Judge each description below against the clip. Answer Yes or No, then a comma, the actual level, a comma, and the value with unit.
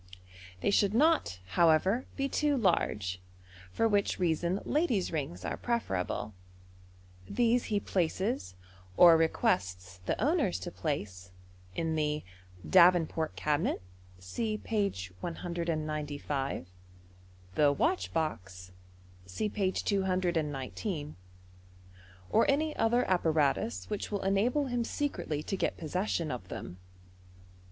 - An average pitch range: No, wide, 7.6 semitones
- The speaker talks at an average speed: No, slow, 115 wpm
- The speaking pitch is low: No, medium, 170 Hz